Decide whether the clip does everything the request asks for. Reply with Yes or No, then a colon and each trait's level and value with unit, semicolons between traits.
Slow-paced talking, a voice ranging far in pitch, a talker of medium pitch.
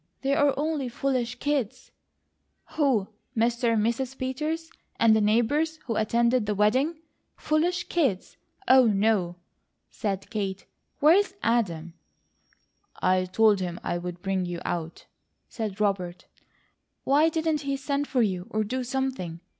No: slow, 130 wpm; wide, 6.0 semitones; high, 235 Hz